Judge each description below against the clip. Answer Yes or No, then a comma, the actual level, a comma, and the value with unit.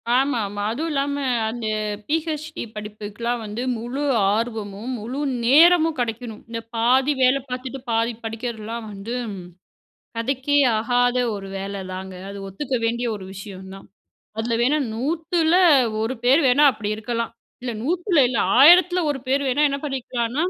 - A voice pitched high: Yes, high, 245 Hz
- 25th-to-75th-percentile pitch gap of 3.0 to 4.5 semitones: Yes, average, 4.2 semitones